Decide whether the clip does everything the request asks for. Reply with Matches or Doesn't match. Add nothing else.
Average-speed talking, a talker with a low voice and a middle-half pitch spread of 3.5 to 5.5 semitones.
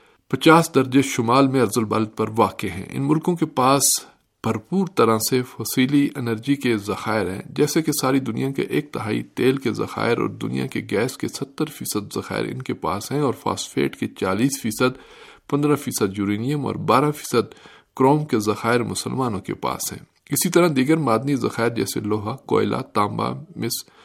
Matches